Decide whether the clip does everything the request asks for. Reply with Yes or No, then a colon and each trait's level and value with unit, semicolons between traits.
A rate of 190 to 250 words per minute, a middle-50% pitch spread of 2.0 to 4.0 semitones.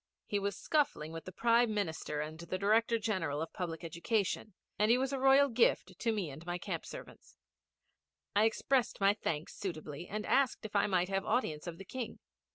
No: average, 195 wpm; wide, 5.4 semitones